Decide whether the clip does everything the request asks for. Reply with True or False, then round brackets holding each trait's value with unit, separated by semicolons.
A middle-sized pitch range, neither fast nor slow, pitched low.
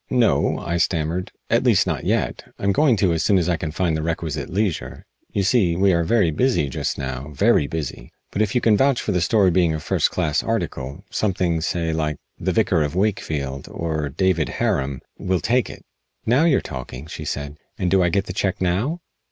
False (4.3 semitones; 210 wpm; 85 Hz)